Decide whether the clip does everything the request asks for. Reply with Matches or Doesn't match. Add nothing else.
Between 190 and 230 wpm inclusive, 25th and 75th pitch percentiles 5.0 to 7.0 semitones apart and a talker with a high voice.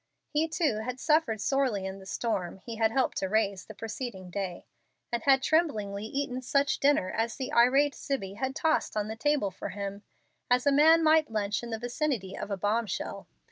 Matches